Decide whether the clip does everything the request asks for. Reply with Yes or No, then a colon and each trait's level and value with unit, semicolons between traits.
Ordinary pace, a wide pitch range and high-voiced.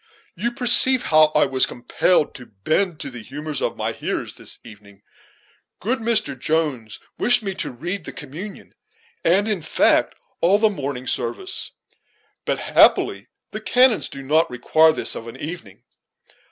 No: average, 155 wpm; wide, 8.2 semitones; medium, 155 Hz